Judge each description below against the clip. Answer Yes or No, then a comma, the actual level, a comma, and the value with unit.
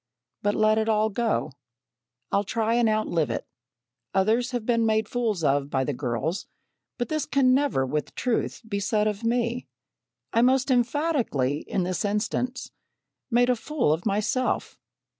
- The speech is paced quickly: No, average, 160 wpm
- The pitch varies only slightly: No, average, 4.2 semitones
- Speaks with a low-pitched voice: No, high, 220 Hz